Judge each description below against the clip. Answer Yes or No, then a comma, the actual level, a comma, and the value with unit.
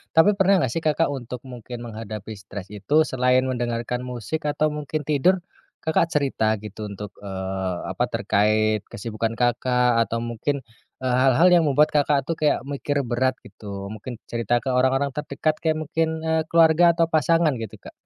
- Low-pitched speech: Yes, low, 130 Hz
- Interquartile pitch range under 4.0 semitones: No, average, 5.3 semitones